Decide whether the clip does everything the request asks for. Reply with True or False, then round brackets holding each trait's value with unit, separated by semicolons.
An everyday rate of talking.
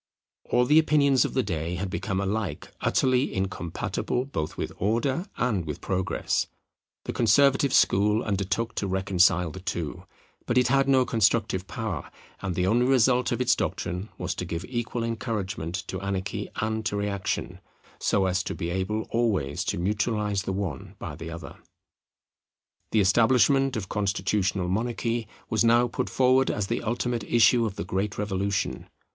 True (160 wpm)